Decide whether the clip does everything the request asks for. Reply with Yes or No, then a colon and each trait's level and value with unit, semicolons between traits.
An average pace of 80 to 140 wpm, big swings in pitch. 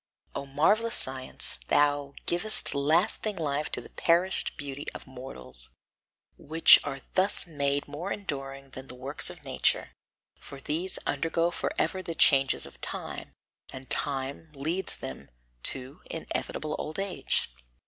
No: slow, 135 wpm; average, 3.7 semitones